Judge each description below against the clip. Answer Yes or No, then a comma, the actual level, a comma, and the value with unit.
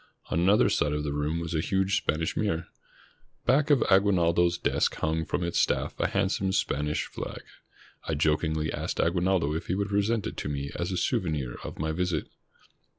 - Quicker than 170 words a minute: Yes, average, 190 wpm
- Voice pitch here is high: No, very low, 85 Hz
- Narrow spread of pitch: No, average, 3.7 semitones